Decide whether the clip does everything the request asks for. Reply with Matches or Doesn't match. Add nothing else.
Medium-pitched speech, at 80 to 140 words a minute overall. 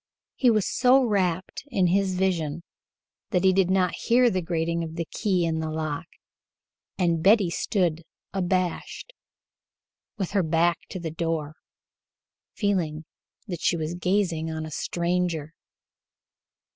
Matches